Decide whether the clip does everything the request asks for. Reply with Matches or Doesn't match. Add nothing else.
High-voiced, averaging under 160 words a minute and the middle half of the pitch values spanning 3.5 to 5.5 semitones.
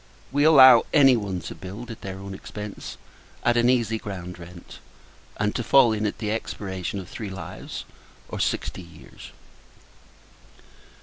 Doesn't match